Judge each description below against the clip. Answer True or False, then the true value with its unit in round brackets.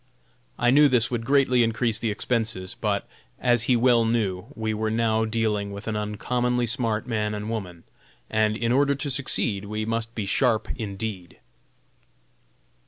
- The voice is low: True (115 Hz)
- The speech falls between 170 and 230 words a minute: False (160 wpm)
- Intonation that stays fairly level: True (2.3 semitones)